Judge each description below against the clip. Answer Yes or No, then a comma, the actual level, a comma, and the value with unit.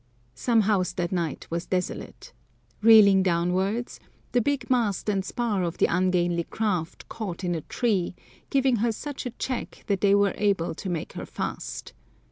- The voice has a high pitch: Yes, high, 195 Hz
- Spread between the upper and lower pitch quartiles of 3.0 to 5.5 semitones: Yes, average, 4.2 semitones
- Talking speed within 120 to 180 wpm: Yes, average, 165 wpm